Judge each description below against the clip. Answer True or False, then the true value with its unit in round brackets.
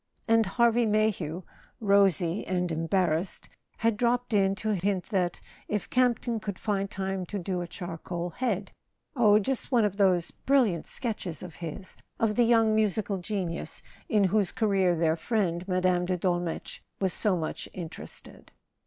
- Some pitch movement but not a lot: True (3.4 semitones)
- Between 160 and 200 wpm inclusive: False (150 wpm)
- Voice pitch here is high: True (195 Hz)